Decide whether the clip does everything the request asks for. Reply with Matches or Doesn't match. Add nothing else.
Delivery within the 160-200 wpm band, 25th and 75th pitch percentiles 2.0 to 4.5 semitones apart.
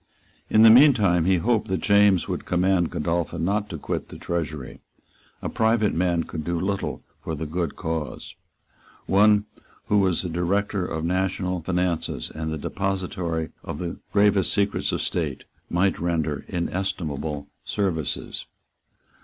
Doesn't match